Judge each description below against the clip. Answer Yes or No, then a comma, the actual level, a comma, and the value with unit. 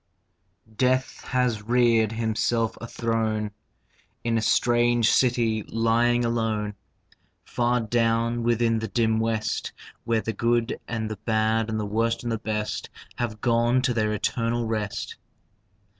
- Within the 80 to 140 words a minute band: Yes, slow, 135 wpm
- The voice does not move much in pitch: Yes, narrow, 1.4 semitones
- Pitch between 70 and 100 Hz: No, low, 115 Hz